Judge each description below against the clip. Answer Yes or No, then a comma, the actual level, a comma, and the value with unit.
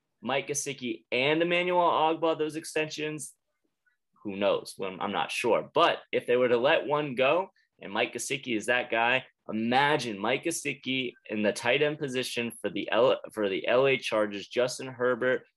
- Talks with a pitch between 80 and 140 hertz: Yes, low, 135 Hz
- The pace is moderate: Yes, average, 170 wpm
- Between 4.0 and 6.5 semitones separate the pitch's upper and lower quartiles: Yes, average, 4.8 semitones